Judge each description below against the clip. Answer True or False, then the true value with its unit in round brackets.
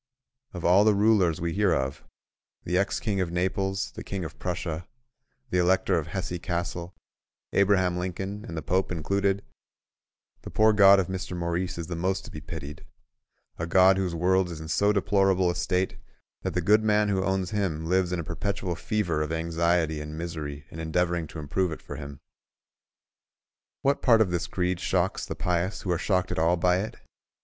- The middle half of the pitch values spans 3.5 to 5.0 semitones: False (2.5 semitones)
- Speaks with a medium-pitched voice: False (90 Hz)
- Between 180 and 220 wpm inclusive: True (185 wpm)